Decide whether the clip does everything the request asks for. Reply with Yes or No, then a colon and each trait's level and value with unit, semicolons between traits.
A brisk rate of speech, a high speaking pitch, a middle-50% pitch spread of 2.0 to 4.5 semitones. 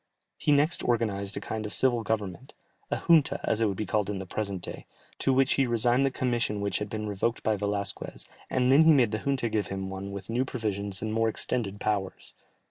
No: fast, 220 wpm; low, 110 Hz; average, 3.6 semitones